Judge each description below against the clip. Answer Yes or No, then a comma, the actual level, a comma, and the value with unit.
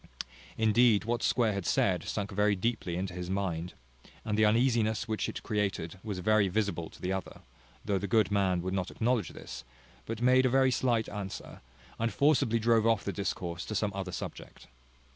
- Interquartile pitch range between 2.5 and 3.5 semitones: Yes, average, 3.1 semitones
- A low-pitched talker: Yes, low, 105 Hz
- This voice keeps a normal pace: Yes, average, 190 wpm